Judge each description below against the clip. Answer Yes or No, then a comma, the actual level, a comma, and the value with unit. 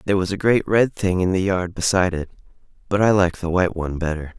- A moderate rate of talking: No, fast, 245 wpm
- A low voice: Yes, very low, 95 Hz